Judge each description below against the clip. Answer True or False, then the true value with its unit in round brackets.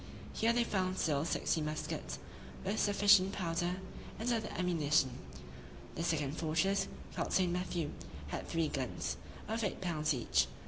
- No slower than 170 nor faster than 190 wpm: False (140 wpm)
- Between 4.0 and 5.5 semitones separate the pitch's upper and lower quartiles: True (4.3 semitones)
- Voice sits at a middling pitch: True (175 Hz)